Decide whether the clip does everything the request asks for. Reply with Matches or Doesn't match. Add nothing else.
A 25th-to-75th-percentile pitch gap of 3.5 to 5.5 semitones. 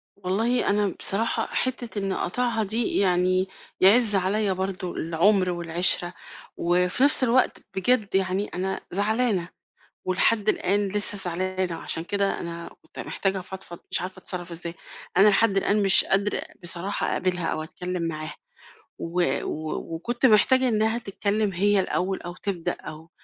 Doesn't match